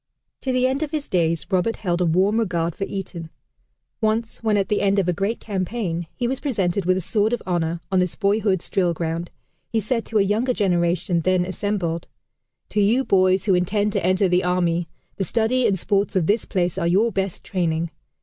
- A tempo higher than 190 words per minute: Yes, fast, 205 wpm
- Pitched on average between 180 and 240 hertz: Yes, high, 190 Hz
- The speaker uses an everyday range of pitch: Yes, average, 3.6 semitones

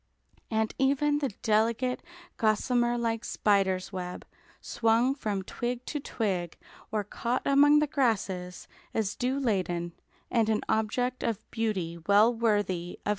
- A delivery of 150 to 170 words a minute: No, slow, 135 wpm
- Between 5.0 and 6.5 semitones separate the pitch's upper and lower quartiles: No, average, 4.0 semitones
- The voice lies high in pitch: Yes, high, 220 Hz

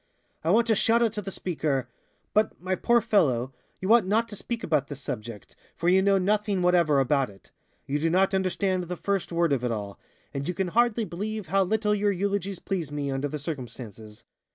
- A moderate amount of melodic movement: No, wide, 6.3 semitones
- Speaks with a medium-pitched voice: Yes, medium, 180 Hz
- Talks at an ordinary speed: No, fast, 210 wpm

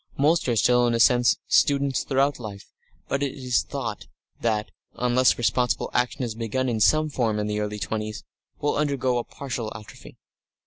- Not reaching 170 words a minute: No, average, 175 wpm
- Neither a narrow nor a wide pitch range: Yes, average, 3.7 semitones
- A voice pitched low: Yes, low, 125 Hz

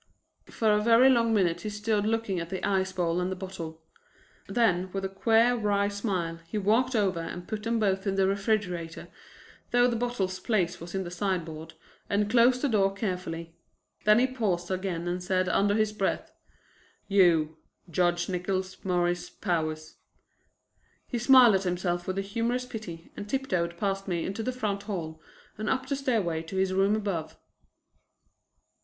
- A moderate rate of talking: Yes, average, 170 wpm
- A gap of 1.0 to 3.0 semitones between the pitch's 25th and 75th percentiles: No, average, 3.7 semitones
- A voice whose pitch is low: No, high, 195 Hz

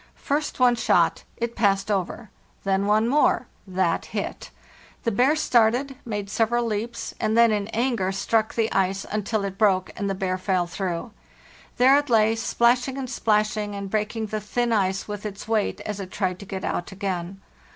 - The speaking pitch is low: No, high, 210 Hz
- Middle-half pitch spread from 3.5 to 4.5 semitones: No, average, 3.1 semitones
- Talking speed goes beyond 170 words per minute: Yes, average, 180 wpm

